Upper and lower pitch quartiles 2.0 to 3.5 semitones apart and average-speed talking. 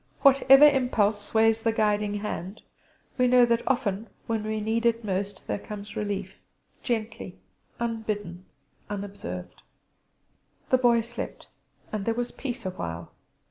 No: narrow, 2.6 semitones; slow, 130 wpm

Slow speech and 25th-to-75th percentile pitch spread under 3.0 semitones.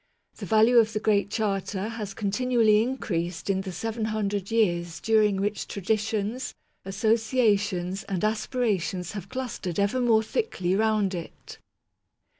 Yes: slow, 130 wpm; narrow, 2.4 semitones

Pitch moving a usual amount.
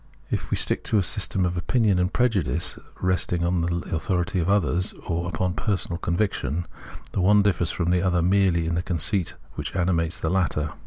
No: narrow, 2.0 semitones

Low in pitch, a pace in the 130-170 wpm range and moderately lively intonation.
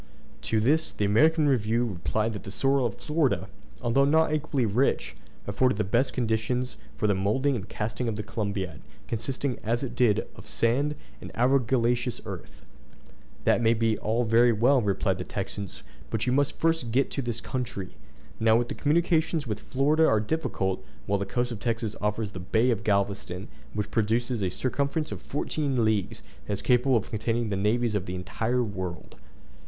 No: low, 115 Hz; average, 180 wpm; average, 3.9 semitones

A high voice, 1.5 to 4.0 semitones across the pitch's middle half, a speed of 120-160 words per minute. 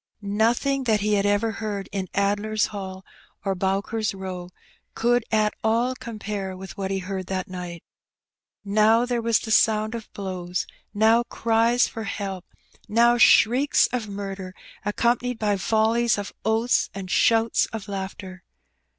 Yes: high, 210 Hz; average, 2.8 semitones; average, 150 wpm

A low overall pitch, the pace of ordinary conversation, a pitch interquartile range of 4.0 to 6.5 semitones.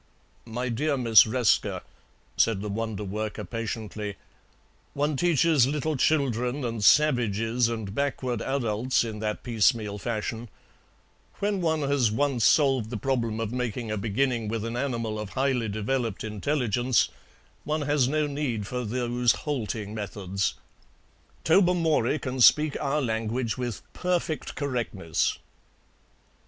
No: low, 120 Hz; slow, 125 wpm; average, 4.3 semitones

